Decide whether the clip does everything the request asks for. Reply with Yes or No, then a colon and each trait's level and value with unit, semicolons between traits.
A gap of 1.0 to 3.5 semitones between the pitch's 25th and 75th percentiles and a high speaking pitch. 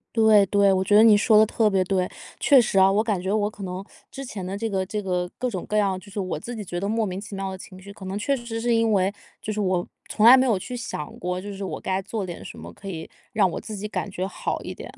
Yes: narrow, 2.6 semitones; high, 200 Hz